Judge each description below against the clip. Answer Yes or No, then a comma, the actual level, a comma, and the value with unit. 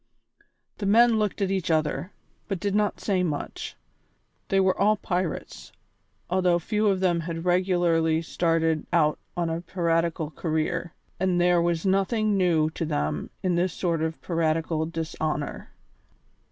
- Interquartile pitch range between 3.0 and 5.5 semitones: No, narrow, 2.6 semitones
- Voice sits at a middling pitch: Yes, medium, 175 Hz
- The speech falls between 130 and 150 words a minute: Yes, average, 145 wpm